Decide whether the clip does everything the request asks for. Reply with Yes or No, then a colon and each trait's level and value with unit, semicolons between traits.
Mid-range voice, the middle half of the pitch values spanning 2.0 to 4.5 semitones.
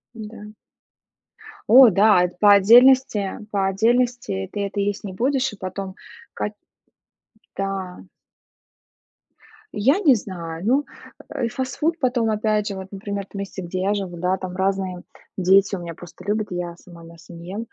No: high, 200 Hz; average, 3.2 semitones